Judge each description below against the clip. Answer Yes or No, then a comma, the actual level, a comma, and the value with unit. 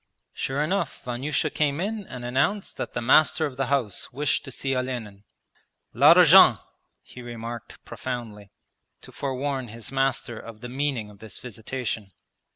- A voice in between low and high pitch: No, low, 125 Hz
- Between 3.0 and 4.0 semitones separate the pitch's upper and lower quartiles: Yes, average, 3.3 semitones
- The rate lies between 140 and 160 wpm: Yes, average, 150 wpm